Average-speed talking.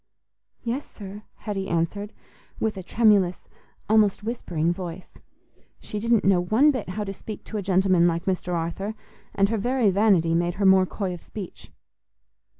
Yes: average, 160 wpm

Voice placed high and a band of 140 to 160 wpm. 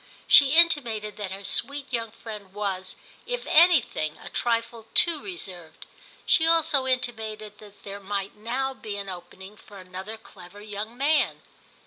Yes: high, 215 Hz; average, 145 wpm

